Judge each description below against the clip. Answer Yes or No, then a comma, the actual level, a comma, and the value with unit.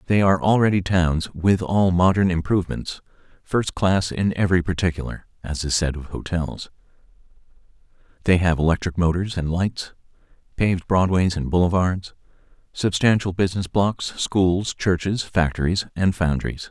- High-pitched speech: No, very low, 90 Hz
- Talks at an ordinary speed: No, slow, 125 wpm